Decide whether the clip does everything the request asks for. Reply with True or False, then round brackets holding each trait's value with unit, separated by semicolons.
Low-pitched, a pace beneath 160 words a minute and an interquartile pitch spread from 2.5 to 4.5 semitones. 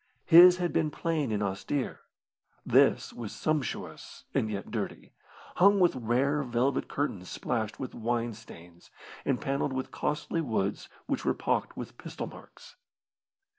False (130 Hz; 140 wpm; 5.4 semitones)